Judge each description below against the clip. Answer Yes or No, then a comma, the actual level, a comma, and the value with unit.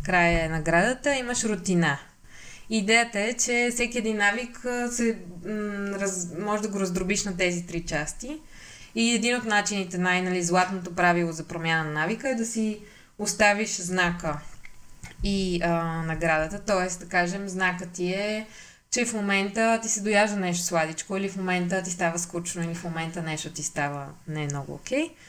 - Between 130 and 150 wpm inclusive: No, fast, 165 wpm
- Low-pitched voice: No, medium, 185 Hz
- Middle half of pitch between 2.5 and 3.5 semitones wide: No, average, 4.0 semitones